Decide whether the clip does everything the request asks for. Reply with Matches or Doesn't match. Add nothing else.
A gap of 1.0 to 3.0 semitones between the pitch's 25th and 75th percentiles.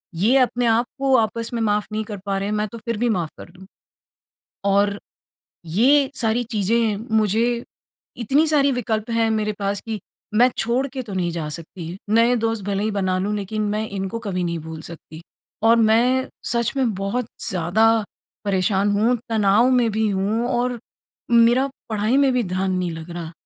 Doesn't match